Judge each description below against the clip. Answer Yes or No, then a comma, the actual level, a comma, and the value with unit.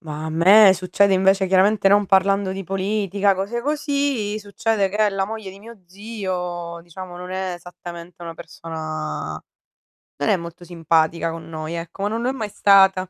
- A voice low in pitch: No, high, 190 Hz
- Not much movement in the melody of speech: No, average, 3.1 semitones